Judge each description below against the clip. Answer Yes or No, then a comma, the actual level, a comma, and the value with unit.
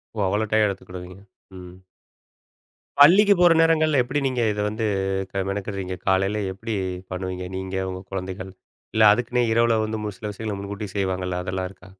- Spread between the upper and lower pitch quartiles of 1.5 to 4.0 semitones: Yes, average, 3.3 semitones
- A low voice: Yes, low, 100 Hz